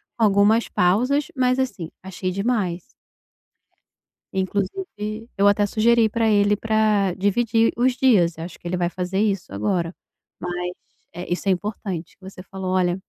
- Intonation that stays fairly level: No, average, 3.5 semitones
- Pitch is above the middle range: Yes, high, 200 Hz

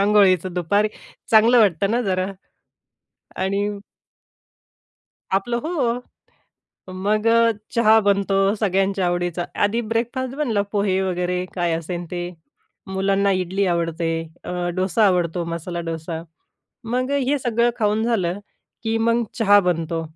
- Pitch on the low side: No, high, 195 Hz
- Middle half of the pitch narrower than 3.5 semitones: No, average, 3.9 semitones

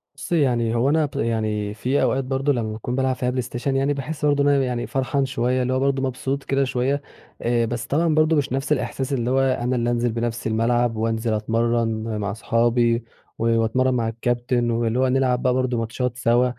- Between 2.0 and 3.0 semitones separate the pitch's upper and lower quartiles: Yes, narrow, 2.4 semitones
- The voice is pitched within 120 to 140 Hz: Yes, low, 125 Hz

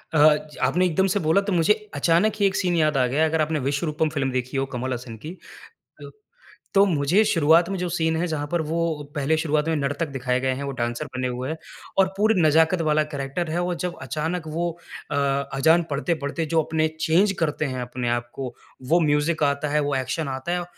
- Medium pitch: Yes, medium, 155 Hz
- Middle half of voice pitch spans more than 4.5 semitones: No, average, 3.5 semitones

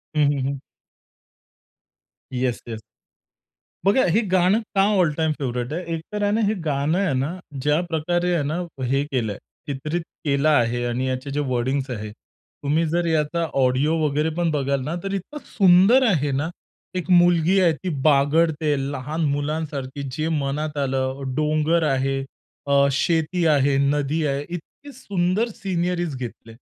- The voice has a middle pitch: Yes, medium, 150 Hz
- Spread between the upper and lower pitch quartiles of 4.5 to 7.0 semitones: No, average, 4.1 semitones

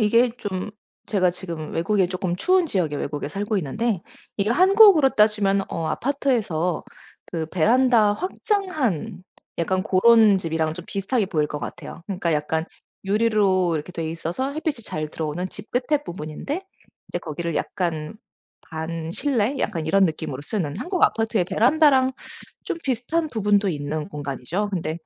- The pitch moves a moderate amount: No, wide, 6.4 semitones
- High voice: Yes, high, 195 Hz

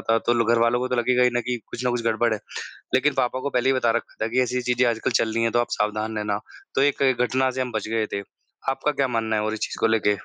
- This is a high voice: No, low, 120 Hz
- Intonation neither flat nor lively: No, narrow, 2.2 semitones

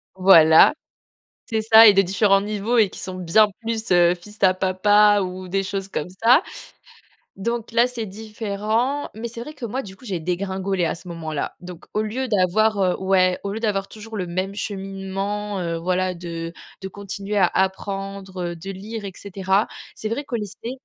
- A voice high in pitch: Yes, high, 195 Hz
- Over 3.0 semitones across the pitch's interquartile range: No, average, 2.7 semitones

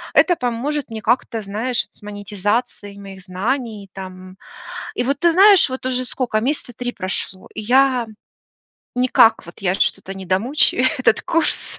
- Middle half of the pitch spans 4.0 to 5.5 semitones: Yes, average, 4.5 semitones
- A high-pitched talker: Yes, high, 230 Hz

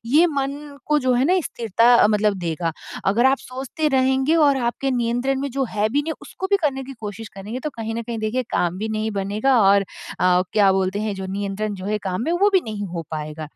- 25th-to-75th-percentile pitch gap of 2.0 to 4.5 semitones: No, average, 5.1 semitones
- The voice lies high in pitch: Yes, high, 225 Hz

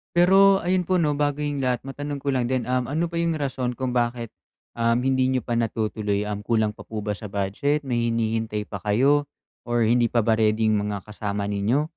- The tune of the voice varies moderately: Yes, average, 4.7 semitones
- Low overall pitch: Yes, low, 120 Hz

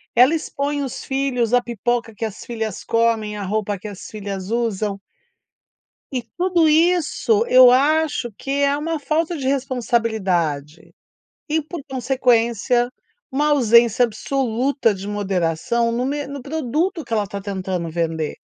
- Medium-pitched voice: No, high, 240 Hz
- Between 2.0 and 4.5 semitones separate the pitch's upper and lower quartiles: No, average, 5.2 semitones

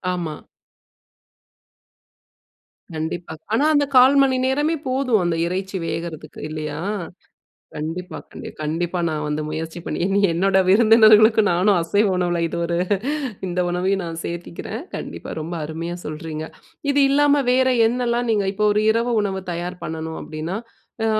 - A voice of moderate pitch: Yes, medium, 180 Hz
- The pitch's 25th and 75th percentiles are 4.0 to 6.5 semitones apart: Yes, average, 5.2 semitones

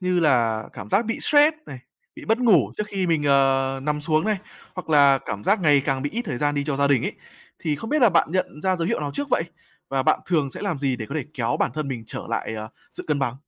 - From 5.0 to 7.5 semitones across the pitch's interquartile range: Yes, wide, 5.5 semitones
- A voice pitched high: No, medium, 150 Hz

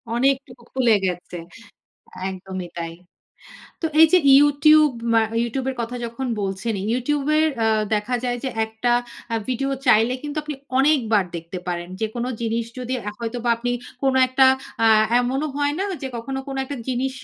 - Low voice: No, high, 245 Hz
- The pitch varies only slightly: No, average, 3.5 semitones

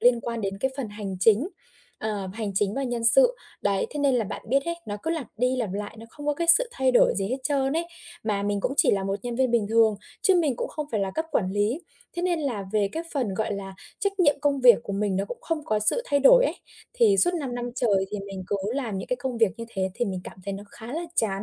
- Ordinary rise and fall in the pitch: No, wide, 5.7 semitones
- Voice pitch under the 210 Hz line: No, high, 235 Hz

